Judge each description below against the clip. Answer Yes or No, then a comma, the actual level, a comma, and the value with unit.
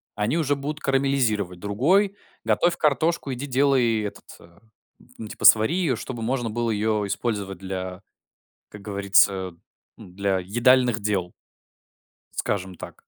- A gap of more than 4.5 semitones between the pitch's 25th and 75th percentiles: Yes, average, 5.3 semitones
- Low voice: Yes, low, 110 Hz